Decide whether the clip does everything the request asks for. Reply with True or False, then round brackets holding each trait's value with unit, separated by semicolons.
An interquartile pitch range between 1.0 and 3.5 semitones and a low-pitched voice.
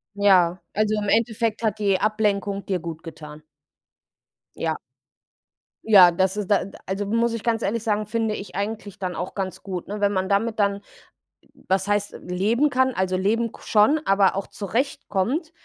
False (2.7 semitones; 205 Hz)